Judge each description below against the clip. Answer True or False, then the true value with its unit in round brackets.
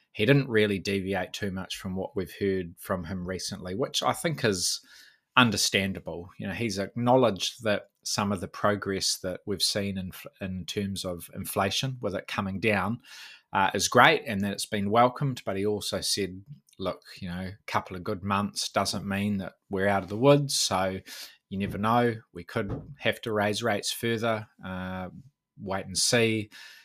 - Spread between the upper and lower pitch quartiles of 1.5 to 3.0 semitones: True (2.6 semitones)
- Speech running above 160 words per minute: True (185 wpm)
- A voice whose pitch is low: True (100 Hz)